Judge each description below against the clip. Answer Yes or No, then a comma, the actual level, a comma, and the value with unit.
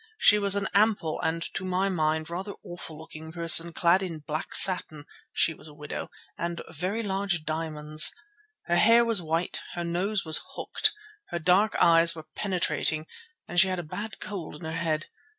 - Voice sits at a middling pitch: Yes, medium, 170 Hz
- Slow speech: No, average, 170 wpm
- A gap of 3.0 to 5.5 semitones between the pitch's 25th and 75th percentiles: Yes, average, 3.3 semitones